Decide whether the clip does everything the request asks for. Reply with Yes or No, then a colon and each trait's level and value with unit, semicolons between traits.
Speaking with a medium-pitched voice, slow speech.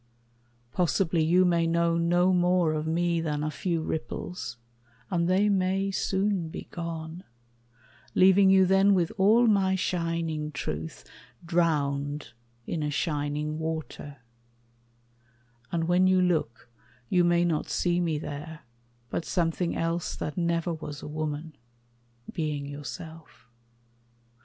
Yes: medium, 170 Hz; slow, 125 wpm